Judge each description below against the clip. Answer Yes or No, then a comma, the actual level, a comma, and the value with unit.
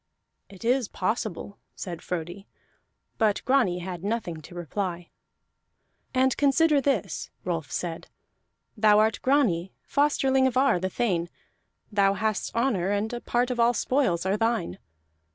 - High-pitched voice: Yes, high, 210 Hz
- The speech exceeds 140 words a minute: No, slow, 135 wpm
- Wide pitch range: Yes, wide, 5.9 semitones